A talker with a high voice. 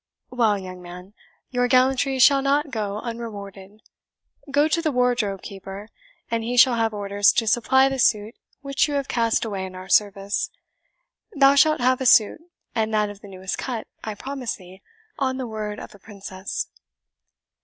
Yes: high, 225 Hz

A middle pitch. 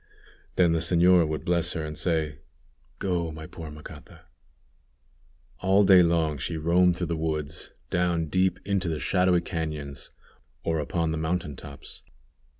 No: very low, 85 Hz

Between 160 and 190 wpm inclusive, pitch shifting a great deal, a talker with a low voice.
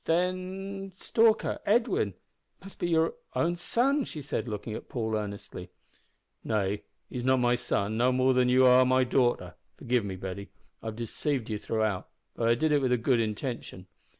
Yes: average, 175 wpm; wide, 6.8 semitones; low, 125 Hz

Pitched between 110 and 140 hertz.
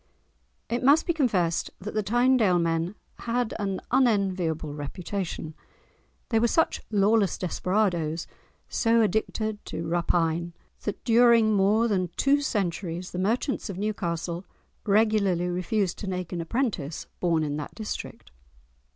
No: high, 195 Hz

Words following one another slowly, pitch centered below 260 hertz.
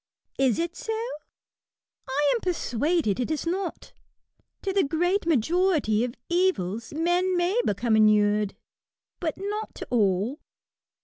No: slow, 125 wpm; very high, 315 Hz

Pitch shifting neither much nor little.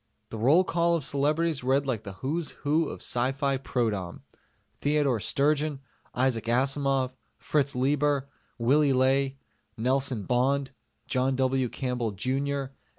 No: narrow, 2.2 semitones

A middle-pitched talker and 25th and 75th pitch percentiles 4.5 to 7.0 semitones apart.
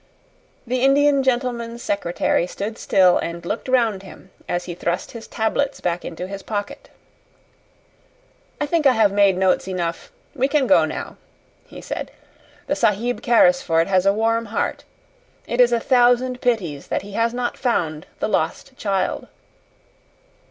No: high, 225 Hz; average, 5.0 semitones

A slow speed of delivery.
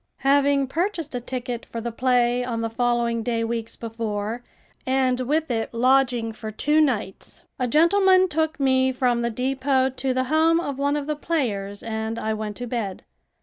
No: average, 180 wpm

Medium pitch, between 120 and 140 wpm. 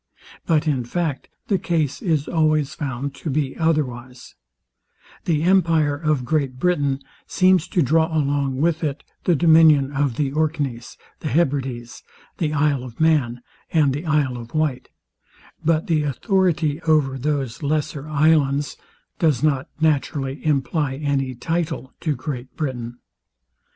Yes: medium, 150 Hz; slow, 135 wpm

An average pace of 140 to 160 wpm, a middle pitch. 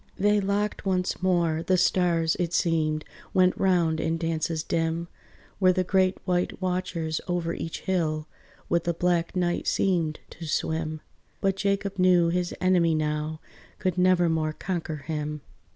Yes: average, 145 wpm; medium, 170 Hz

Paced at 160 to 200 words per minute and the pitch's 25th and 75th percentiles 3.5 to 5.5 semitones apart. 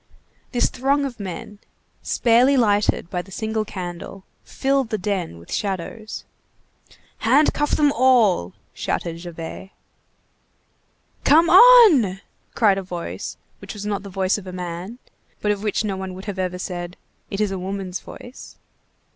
No: average, 145 wpm; average, 4.6 semitones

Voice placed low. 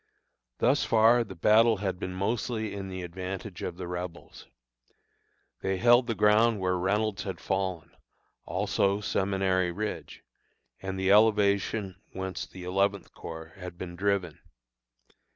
Yes: very low, 95 Hz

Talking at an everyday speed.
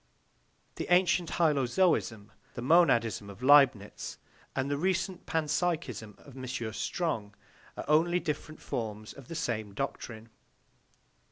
No: slow, 115 wpm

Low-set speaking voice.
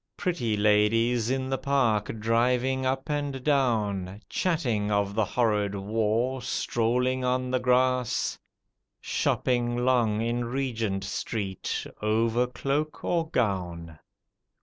Yes: low, 120 Hz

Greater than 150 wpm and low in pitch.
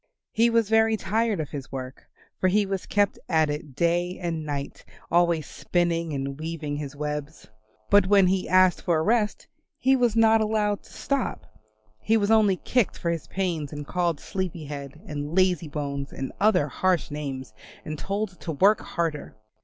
No: average, 175 wpm; medium, 175 Hz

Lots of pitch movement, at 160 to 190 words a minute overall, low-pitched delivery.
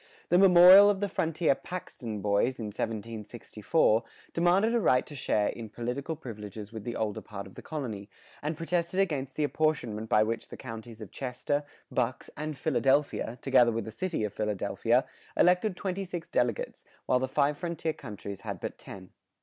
Yes: wide, 7.2 semitones; average, 175 wpm; low, 130 Hz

